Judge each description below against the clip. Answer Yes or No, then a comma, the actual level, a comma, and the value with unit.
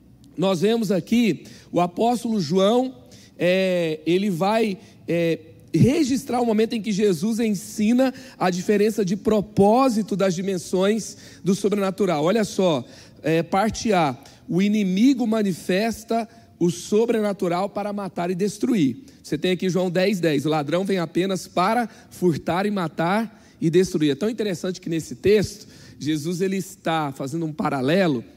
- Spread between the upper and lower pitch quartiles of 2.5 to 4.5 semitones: Yes, average, 4.0 semitones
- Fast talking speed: No, average, 140 wpm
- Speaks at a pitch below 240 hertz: Yes, high, 190 Hz